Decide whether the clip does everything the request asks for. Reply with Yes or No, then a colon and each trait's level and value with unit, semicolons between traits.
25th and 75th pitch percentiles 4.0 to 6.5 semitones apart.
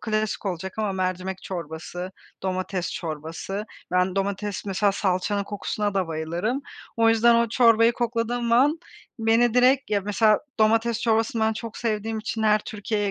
No: average, 3.2 semitones